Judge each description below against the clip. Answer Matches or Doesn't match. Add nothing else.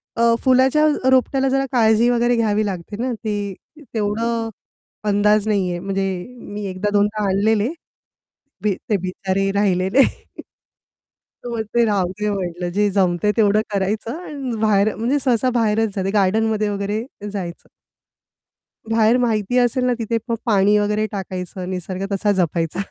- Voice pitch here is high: Matches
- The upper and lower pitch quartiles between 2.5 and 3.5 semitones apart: Matches